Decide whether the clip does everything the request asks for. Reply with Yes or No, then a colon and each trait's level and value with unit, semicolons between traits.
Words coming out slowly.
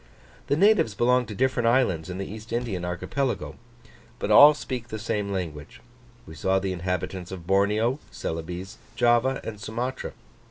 No: average, 155 wpm